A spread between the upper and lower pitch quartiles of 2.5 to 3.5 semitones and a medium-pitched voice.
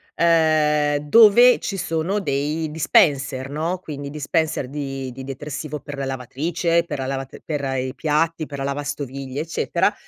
Yes: average, 2.8 semitones; medium, 150 Hz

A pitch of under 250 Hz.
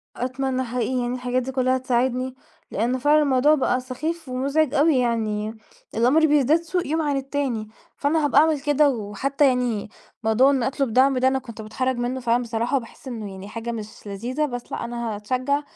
No: very high, 255 Hz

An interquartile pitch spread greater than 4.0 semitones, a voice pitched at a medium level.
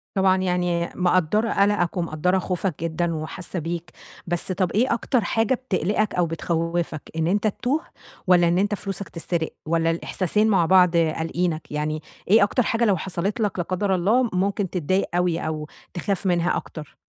No: average, 3.1 semitones; medium, 180 Hz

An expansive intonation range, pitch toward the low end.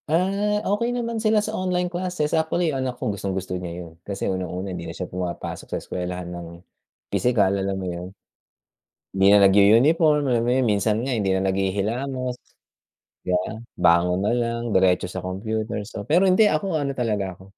Yes: wide, 8.9 semitones; low, 110 Hz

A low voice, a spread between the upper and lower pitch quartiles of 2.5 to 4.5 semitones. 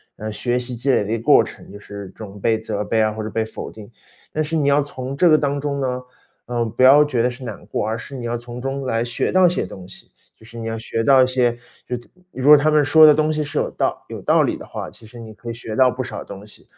Yes: low, 120 Hz; average, 3.9 semitones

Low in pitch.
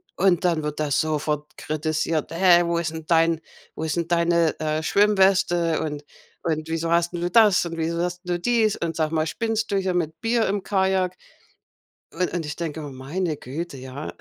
No: medium, 170 Hz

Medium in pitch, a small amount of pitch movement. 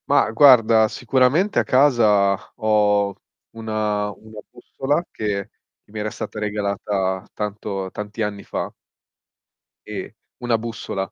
No: low, 105 Hz; narrow, 2.1 semitones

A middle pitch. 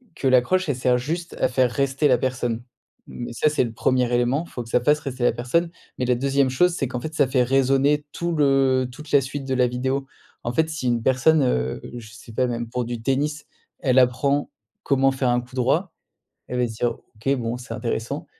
No: low, 130 Hz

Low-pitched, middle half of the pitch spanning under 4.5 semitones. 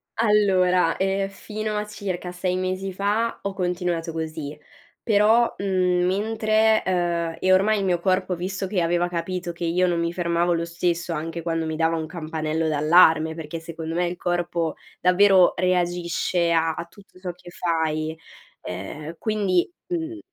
No: medium, 175 Hz; narrow, 2.5 semitones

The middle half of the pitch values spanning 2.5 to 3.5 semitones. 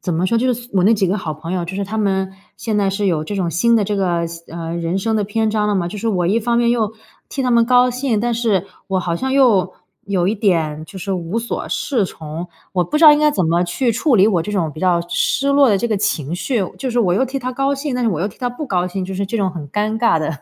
No: average, 4.9 semitones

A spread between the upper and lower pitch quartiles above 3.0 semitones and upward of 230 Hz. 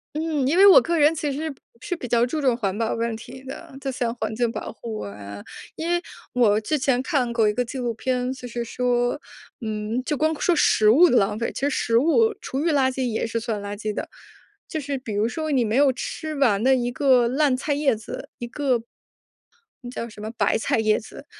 Yes: average, 4.2 semitones; very high, 250 Hz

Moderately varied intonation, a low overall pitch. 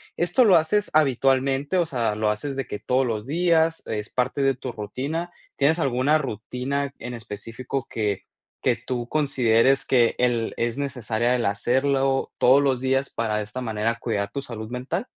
Yes: average, 3.5 semitones; low, 130 Hz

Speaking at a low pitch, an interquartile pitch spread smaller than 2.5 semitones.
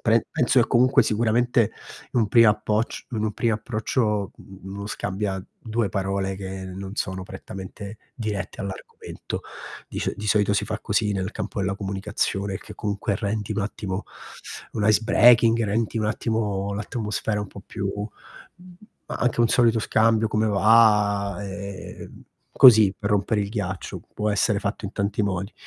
Yes: low, 105 Hz; narrow, 2.0 semitones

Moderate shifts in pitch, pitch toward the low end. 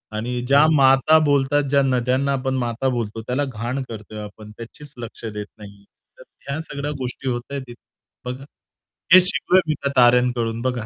Yes: average, 3.1 semitones; low, 125 Hz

